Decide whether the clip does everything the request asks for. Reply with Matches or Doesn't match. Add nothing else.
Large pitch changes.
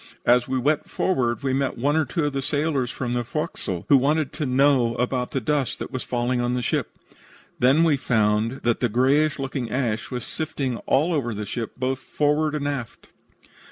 Doesn't match